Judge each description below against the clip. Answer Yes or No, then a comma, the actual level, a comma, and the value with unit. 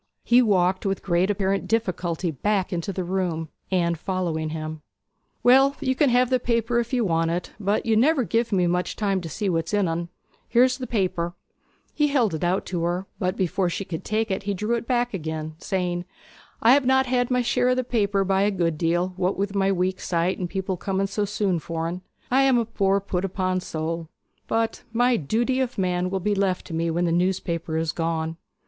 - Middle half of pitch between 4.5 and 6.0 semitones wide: Yes, average, 4.8 semitones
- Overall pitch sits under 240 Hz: Yes, high, 190 Hz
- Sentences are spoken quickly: Yes, fast, 210 wpm